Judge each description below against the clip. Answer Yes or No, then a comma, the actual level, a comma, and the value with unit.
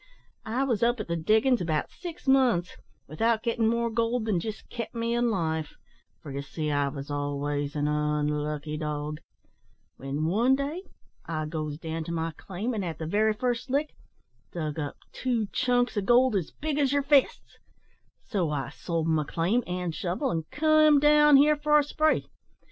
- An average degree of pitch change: No, wide, 8.2 semitones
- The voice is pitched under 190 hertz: No, high, 200 Hz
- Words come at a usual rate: Yes, average, 180 wpm